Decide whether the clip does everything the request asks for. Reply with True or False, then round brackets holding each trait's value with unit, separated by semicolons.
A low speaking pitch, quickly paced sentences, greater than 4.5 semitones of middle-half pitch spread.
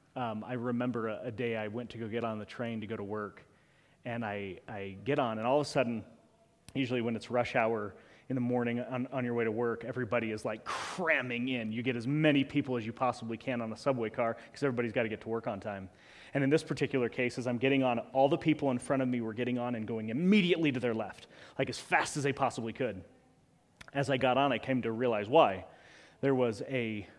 False (120 Hz; 250 wpm; 2.8 semitones)